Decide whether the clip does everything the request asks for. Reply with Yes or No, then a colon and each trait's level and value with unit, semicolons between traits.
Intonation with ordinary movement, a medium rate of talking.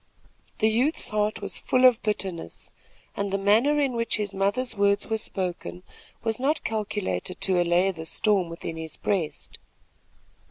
Yes: average, 3.5 semitones; average, 155 wpm